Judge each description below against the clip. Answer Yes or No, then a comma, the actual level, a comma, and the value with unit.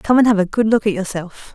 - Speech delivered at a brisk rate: Yes, fast, 310 wpm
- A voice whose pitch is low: No, high, 205 Hz